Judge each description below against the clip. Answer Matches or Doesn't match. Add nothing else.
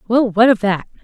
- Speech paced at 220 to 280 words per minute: Matches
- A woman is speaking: Matches